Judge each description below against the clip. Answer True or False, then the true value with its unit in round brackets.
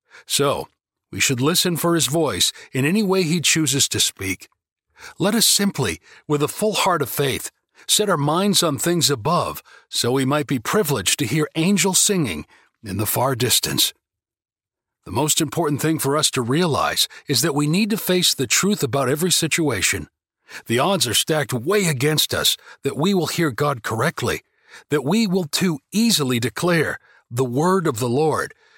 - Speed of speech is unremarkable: True (175 wpm)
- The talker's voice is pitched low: False (155 Hz)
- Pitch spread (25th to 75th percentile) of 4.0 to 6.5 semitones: True (5.3 semitones)